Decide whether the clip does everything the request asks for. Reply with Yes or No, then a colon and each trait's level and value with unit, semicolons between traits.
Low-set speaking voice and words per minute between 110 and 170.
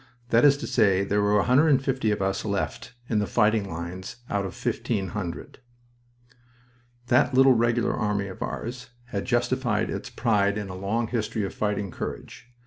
Yes: low, 105 Hz; average, 160 wpm